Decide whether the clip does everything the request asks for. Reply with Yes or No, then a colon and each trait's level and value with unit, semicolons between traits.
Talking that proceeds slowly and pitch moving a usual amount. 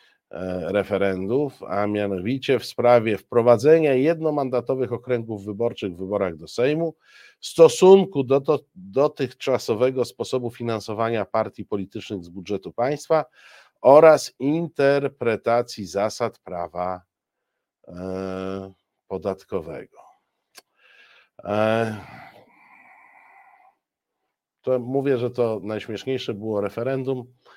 Yes: slow, 85 wpm; average, 4.9 semitones